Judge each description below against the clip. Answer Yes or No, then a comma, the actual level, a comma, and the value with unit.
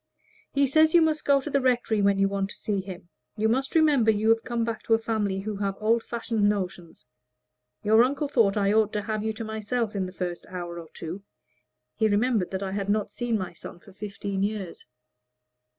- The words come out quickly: Yes, fast, 215 wpm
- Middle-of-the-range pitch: No, high, 215 Hz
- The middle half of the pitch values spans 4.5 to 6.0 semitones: No, average, 3.0 semitones